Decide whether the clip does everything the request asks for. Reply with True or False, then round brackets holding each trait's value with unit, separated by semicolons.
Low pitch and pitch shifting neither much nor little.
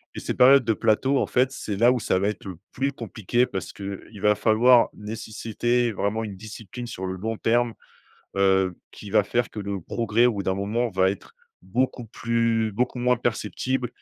True (110 Hz; 3.2 semitones)